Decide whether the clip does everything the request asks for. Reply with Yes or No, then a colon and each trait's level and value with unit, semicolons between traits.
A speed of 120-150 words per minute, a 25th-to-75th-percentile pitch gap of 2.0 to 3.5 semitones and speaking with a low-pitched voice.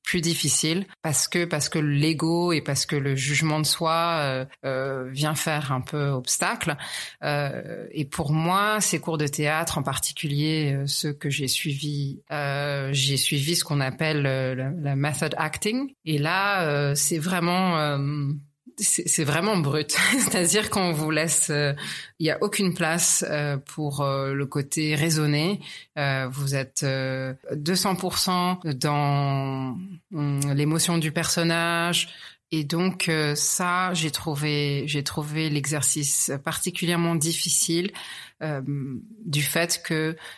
No: slow, 145 wpm; average, 2.9 semitones; medium, 155 Hz